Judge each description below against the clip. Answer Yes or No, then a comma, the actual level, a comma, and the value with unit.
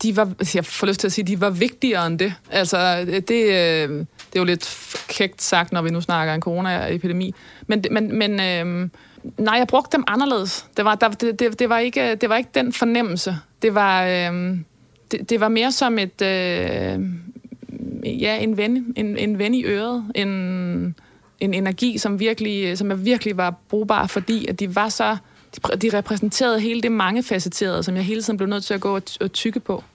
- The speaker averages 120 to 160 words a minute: No, average, 190 wpm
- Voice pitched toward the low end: No, high, 205 Hz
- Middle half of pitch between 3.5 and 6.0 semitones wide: Yes, average, 3.8 semitones